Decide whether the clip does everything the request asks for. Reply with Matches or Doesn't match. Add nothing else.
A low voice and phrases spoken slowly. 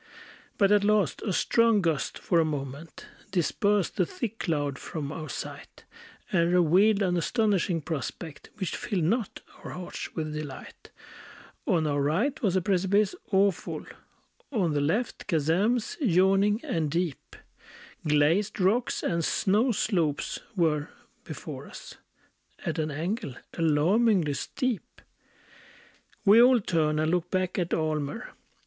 Doesn't match